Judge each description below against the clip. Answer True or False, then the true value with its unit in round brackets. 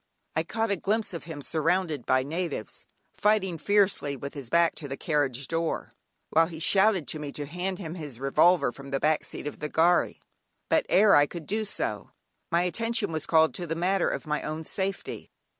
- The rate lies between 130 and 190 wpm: False (200 wpm)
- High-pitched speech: False (165 Hz)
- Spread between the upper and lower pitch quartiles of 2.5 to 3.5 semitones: False (4.1 semitones)